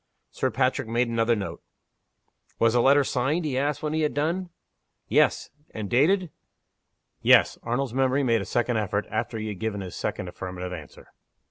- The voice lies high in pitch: No, low, 120 Hz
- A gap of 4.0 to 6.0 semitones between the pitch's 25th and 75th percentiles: Yes, average, 4.8 semitones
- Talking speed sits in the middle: Yes, average, 170 wpm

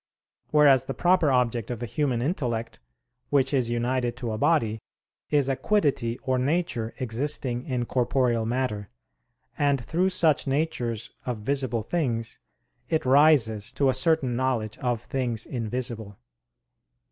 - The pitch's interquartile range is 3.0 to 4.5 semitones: Yes, average, 3.4 semitones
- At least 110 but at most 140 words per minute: Yes, slow, 135 wpm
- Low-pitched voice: Yes, low, 125 Hz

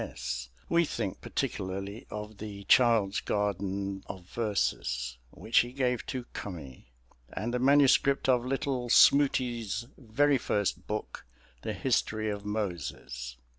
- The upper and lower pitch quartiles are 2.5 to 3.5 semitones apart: No, average, 4.3 semitones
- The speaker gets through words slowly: Yes, slow, 125 wpm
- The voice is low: Yes, low, 105 Hz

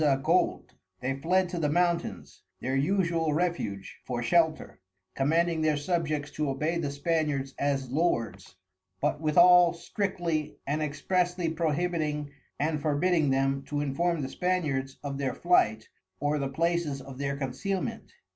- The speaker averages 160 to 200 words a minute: No, average, 140 wpm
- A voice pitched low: No, medium, 150 Hz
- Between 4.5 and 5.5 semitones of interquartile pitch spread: No, average, 3.8 semitones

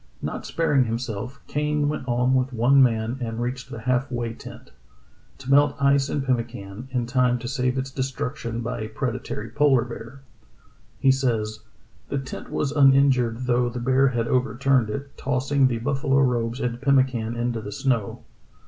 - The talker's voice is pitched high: No, low, 125 Hz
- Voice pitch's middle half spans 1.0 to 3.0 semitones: Yes, narrow, 2.4 semitones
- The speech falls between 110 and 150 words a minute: No, average, 165 wpm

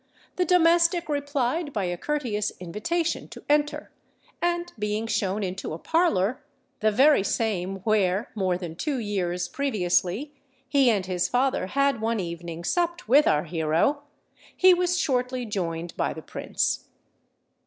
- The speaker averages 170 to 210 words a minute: No, slow, 135 wpm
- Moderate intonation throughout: No, wide, 8.1 semitones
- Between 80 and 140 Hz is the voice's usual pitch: No, high, 225 Hz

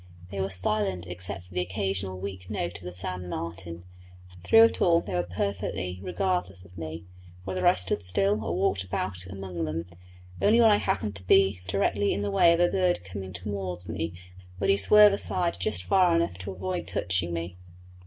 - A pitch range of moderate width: No, narrow, 2.0 semitones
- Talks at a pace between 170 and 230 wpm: Yes, average, 195 wpm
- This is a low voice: Yes, very low, 95 Hz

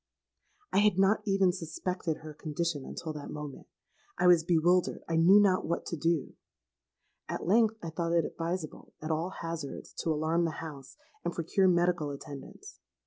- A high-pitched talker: No, medium, 170 Hz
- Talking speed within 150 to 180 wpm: Yes, average, 160 wpm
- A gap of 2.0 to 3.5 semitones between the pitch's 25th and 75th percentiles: Yes, narrow, 2.5 semitones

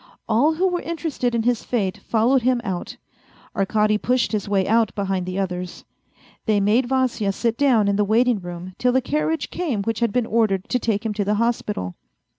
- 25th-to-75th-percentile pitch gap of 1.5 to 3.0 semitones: No, average, 3.8 semitones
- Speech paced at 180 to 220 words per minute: Yes, average, 200 wpm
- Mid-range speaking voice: No, high, 225 Hz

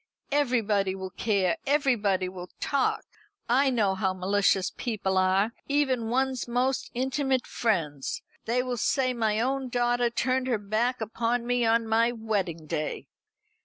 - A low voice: No, high, 230 Hz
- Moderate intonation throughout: Yes, average, 4.4 semitones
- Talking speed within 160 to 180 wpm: No, average, 140 wpm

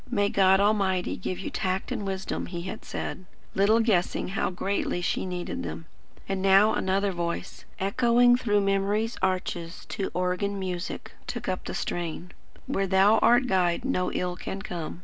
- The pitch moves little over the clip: Yes, narrow, 2.0 semitones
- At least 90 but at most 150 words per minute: No, average, 165 wpm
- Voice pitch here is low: No, high, 190 Hz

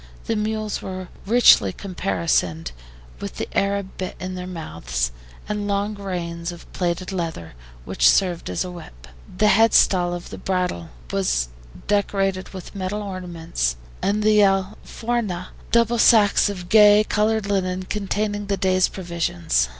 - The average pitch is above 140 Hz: Yes, medium, 185 Hz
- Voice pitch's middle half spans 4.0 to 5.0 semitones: No, average, 3.3 semitones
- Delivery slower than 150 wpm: Yes, average, 140 wpm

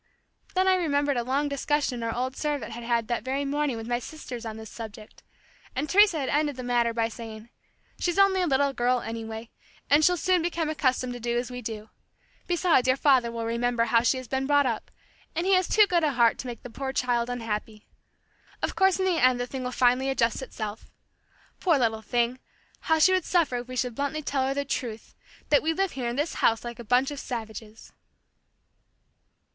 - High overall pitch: Yes, very high, 255 Hz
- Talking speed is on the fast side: Yes, fast, 215 wpm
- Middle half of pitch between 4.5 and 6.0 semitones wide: No, average, 3.9 semitones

